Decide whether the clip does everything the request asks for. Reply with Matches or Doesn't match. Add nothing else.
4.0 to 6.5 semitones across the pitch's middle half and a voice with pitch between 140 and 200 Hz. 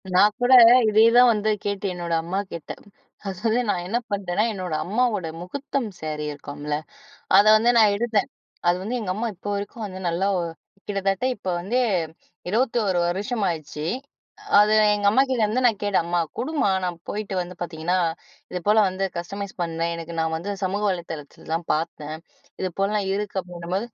Doesn't match